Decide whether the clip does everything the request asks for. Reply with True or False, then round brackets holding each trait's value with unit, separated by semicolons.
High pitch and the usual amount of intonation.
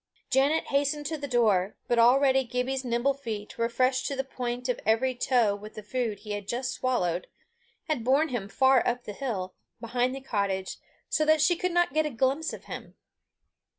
True (250 Hz; 3.5 semitones)